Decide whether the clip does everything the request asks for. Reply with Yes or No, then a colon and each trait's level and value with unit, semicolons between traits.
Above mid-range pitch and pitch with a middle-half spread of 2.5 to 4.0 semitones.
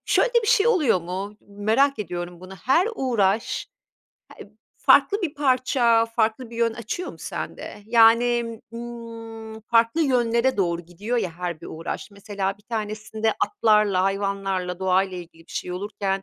Yes: high, 220 Hz; average, 3.6 semitones